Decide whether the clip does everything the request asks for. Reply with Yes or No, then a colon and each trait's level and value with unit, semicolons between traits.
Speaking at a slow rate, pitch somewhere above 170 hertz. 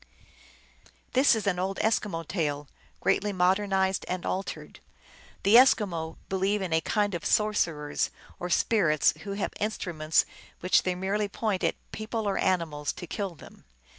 No: average, 145 wpm; high, 190 Hz